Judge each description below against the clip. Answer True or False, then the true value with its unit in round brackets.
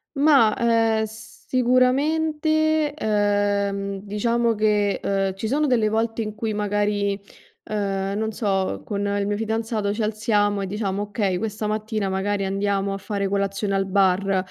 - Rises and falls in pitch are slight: True (2.1 semitones)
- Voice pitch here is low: False (210 Hz)